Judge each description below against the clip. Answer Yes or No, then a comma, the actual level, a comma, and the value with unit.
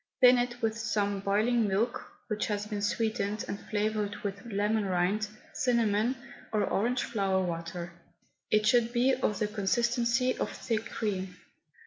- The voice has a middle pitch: No, high, 215 Hz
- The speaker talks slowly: No, average, 145 wpm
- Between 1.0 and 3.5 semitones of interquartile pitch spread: Yes, average, 2.8 semitones